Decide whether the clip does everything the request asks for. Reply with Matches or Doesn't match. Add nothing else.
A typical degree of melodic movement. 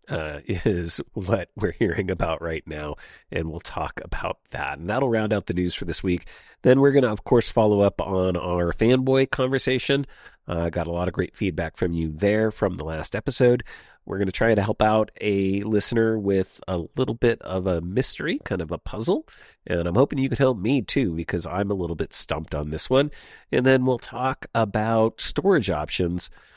Doesn't match